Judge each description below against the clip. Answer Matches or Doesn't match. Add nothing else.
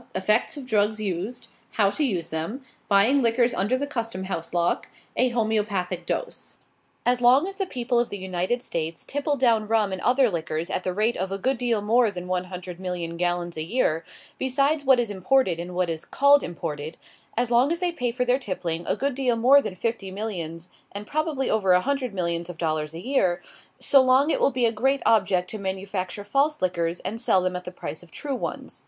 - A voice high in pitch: Matches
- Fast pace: Matches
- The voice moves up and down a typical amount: Doesn't match